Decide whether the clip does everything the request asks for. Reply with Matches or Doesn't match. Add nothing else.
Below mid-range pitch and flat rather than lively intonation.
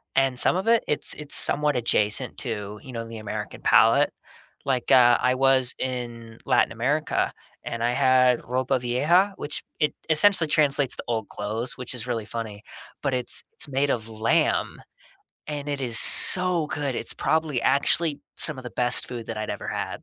Doesn't match